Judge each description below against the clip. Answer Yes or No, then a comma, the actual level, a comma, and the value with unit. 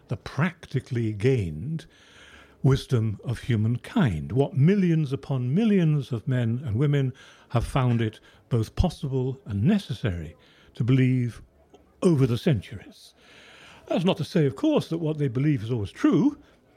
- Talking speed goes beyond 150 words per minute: No, average, 140 wpm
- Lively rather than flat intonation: No, average, 4.6 semitones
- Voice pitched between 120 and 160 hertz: Yes, low, 135 Hz